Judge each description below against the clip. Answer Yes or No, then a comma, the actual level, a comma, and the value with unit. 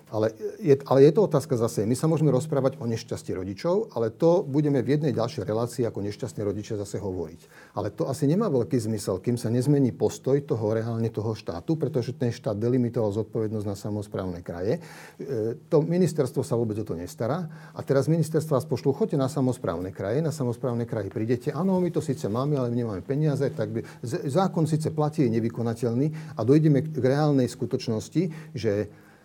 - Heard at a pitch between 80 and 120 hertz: No, low, 130 Hz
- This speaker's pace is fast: Yes, fast, 185 wpm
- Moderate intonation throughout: Yes, average, 4.6 semitones